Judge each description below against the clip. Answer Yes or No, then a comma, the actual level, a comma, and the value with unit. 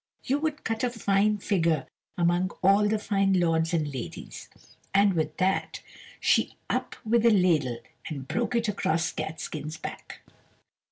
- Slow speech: No, average, 150 wpm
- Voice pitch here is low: No, high, 190 Hz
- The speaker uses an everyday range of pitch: Yes, average, 4.7 semitones